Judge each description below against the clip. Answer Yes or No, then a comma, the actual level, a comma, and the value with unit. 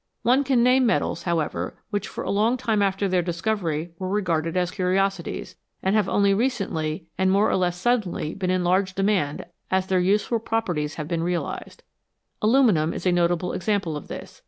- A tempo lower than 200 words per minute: Yes, average, 180 wpm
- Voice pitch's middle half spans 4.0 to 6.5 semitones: No, average, 3.4 semitones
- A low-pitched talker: No, high, 190 Hz